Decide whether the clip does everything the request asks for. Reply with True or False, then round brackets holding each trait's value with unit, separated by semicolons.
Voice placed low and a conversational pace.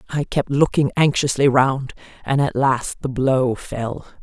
True (130 Hz; 155 wpm)